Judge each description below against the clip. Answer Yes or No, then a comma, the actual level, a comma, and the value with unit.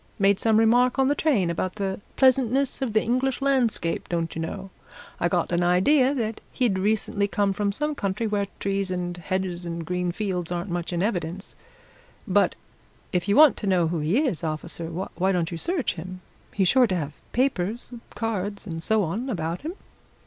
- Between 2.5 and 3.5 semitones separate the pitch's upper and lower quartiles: No, average, 4.7 semitones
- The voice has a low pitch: No, high, 195 Hz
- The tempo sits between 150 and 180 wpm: No, average, 190 wpm